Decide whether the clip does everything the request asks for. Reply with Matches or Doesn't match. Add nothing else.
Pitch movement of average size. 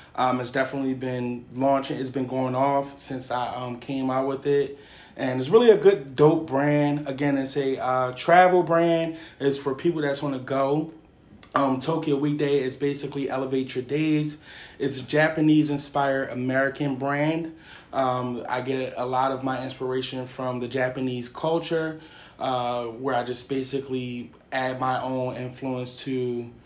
Doesn't match